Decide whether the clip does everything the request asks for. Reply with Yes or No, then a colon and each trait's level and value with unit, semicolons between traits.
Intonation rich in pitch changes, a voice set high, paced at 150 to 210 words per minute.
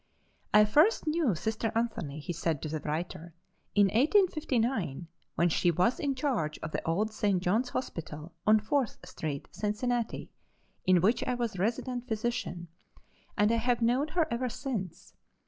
Yes: wide, 6.1 semitones; high, 220 Hz; average, 155 wpm